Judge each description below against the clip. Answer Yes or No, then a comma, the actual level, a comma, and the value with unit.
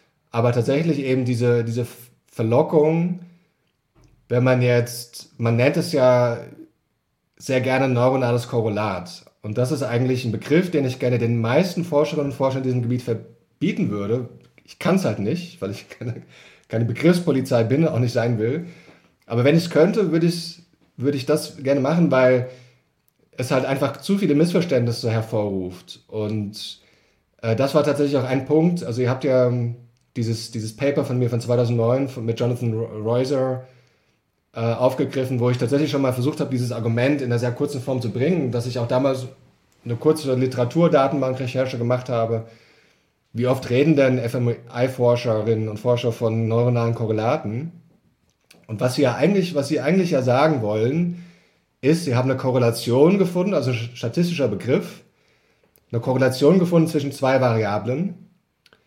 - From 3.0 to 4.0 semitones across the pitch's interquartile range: Yes, average, 3.7 semitones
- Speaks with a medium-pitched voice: No, low, 130 Hz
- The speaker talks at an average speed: Yes, average, 160 wpm